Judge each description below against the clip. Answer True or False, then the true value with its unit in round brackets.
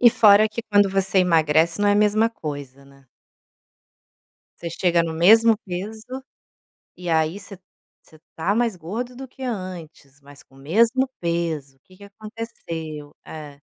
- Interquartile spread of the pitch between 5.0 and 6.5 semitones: True (5.4 semitones)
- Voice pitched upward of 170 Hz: True (185 Hz)